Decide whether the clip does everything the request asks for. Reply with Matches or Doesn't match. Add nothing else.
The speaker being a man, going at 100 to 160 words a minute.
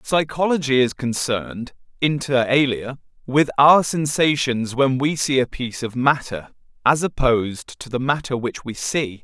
Matches